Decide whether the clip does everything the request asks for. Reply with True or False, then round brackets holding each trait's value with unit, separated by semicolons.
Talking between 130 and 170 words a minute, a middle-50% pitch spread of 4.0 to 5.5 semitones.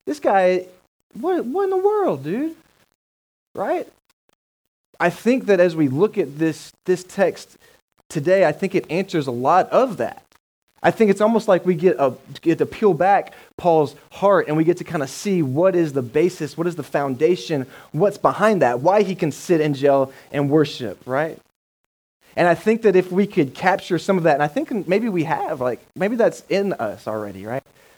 False (200 wpm; 4.8 semitones)